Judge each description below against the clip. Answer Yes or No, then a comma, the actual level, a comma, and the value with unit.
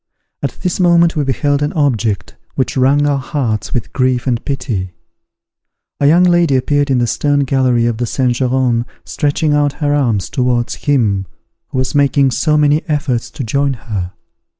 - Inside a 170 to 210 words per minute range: Yes, average, 175 wpm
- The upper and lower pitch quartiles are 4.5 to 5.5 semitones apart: No, average, 3.3 semitones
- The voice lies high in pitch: No, low, 135 Hz